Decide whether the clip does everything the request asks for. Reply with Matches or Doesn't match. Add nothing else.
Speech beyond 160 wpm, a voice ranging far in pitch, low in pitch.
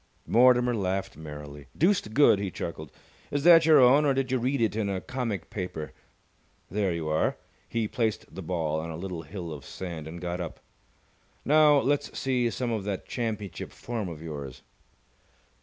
Matches